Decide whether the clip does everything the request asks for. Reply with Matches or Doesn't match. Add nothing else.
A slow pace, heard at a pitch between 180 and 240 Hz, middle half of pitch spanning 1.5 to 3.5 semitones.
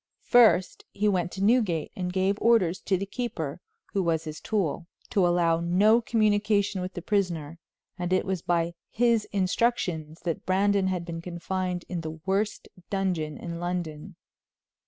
Doesn't match